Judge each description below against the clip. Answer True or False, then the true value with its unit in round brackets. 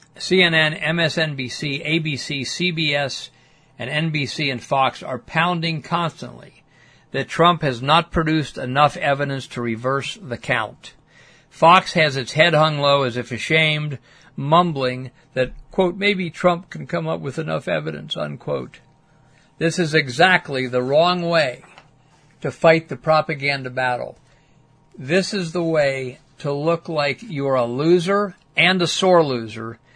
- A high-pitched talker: False (155 Hz)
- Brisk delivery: False (135 wpm)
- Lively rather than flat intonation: False (3.8 semitones)